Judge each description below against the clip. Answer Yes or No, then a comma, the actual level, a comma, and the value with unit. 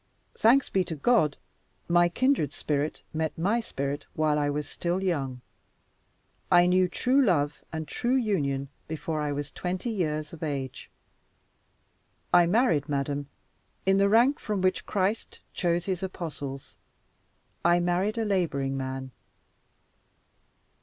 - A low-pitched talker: No, medium, 170 Hz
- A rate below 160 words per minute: Yes, slow, 135 wpm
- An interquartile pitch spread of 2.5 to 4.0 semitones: No, average, 4.9 semitones